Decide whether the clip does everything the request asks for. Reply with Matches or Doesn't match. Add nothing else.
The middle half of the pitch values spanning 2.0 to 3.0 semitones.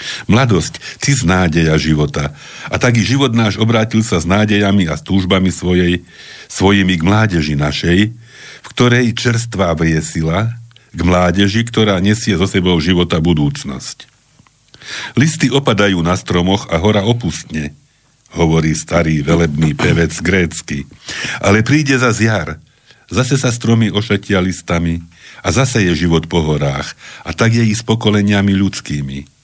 Doesn't match